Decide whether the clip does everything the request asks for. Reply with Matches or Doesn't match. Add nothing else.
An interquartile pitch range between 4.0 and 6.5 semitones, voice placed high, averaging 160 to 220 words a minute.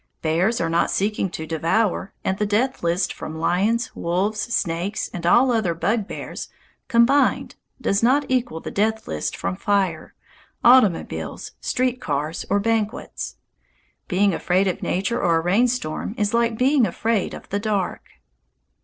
Doesn't match